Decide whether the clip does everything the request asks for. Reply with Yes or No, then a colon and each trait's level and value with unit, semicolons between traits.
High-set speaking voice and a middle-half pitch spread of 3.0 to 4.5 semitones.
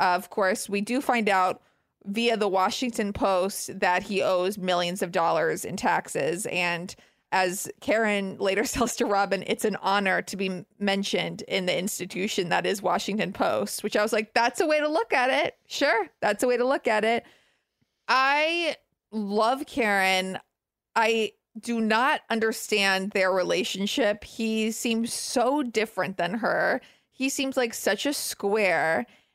Yes: high, 210 Hz; average, 3.5 semitones